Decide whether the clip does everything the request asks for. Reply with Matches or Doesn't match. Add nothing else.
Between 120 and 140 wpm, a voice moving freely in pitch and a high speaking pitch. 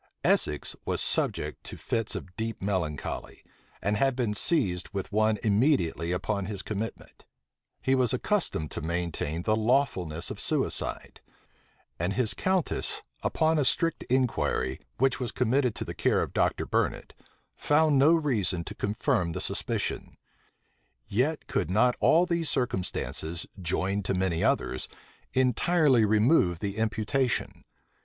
Doesn't match